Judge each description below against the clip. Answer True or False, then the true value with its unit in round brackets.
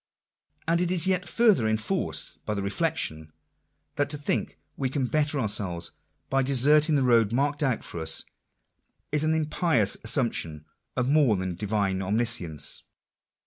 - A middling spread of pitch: False (7.1 semitones)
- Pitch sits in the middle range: False (125 Hz)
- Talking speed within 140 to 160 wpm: True (150 wpm)